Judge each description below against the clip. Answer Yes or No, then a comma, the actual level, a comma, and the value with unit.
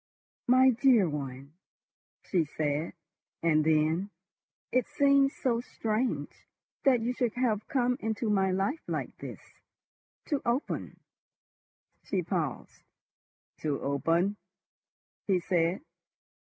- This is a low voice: No, high, 200 Hz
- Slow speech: Yes, slow, 100 wpm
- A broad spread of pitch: Yes, wide, 7.5 semitones